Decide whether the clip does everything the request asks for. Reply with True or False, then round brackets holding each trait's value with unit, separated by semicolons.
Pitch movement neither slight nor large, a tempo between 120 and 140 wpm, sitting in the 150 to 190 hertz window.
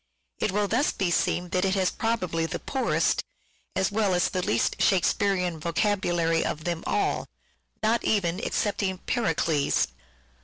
False (3.4 semitones; 150 wpm; 185 Hz)